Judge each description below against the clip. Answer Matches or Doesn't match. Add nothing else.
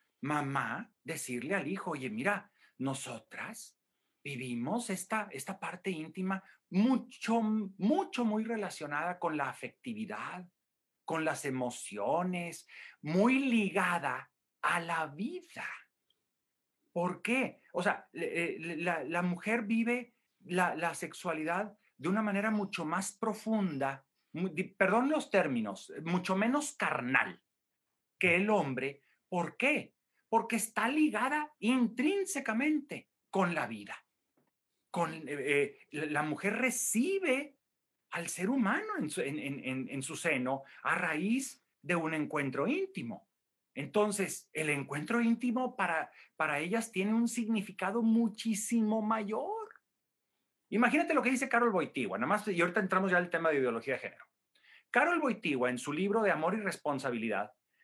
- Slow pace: Matches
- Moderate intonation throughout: Doesn't match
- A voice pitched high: Matches